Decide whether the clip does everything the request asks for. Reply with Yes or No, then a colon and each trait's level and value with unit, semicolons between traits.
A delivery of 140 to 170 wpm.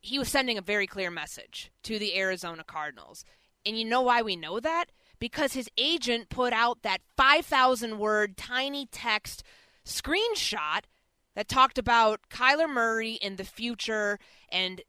Yes: average, 155 wpm